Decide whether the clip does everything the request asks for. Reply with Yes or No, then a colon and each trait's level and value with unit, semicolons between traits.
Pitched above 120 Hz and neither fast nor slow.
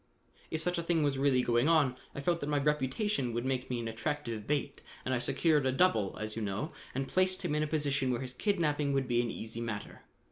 No: low, 135 Hz; fast, 240 wpm